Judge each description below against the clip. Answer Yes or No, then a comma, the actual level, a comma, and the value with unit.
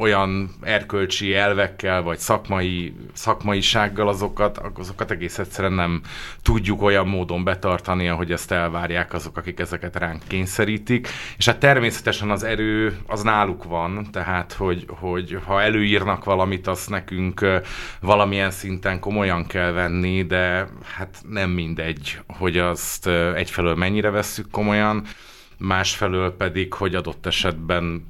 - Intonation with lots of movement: No, narrow, 2.5 semitones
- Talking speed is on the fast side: No, average, 125 wpm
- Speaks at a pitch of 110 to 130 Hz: No, very low, 95 Hz